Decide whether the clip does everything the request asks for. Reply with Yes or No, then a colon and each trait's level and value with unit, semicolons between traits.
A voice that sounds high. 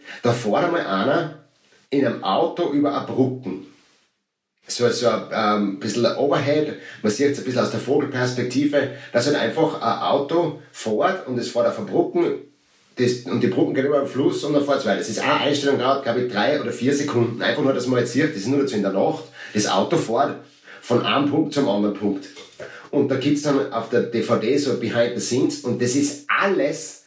No: low, 135 Hz